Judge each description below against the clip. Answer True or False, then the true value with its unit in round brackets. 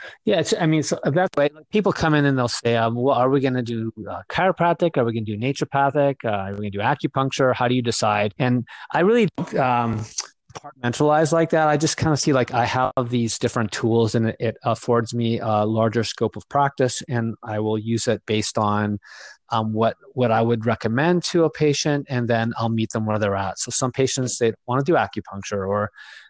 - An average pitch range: True (4.4 semitones)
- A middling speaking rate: False (230 wpm)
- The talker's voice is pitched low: True (120 Hz)